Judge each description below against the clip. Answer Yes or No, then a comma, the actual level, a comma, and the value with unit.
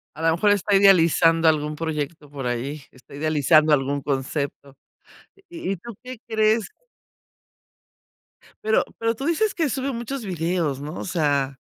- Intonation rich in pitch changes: Yes, wide, 7.0 semitones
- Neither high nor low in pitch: Yes, medium, 165 Hz